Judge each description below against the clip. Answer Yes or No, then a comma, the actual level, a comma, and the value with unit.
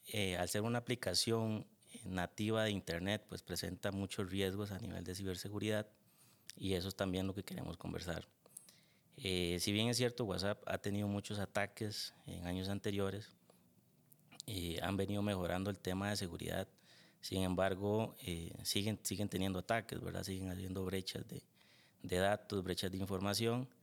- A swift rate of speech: No, average, 155 wpm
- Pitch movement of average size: No, narrow, 2.3 semitones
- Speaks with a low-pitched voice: Yes, low, 100 Hz